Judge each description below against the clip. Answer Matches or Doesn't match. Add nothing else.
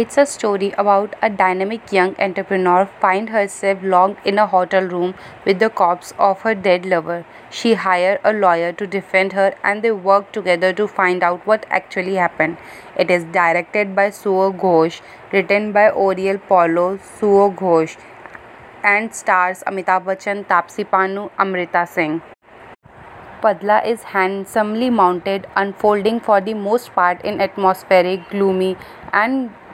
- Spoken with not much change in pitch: Matches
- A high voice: Matches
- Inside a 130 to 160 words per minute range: Matches